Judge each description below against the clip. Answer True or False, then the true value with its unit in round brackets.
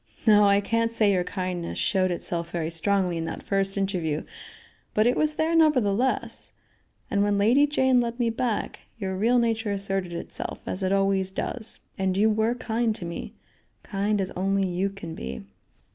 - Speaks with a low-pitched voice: False (200 Hz)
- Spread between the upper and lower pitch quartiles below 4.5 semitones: True (3.6 semitones)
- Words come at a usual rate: True (175 wpm)